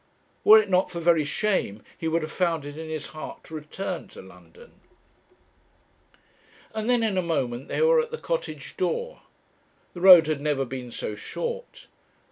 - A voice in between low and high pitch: Yes, medium, 170 Hz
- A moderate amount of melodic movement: No, wide, 6.5 semitones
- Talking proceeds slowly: No, average, 175 wpm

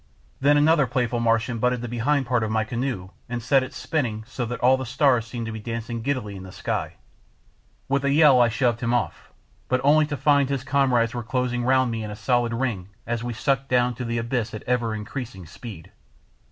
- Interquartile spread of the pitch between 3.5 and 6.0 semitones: No, narrow, 2.5 semitones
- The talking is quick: Yes, fast, 220 wpm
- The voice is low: Yes, low, 120 Hz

